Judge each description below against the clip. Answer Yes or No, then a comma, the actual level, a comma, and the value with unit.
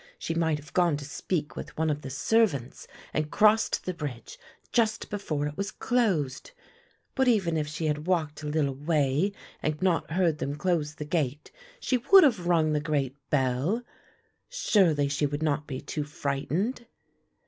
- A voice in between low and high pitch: Yes, medium, 155 Hz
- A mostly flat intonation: No, average, 4.2 semitones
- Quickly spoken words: No, average, 170 wpm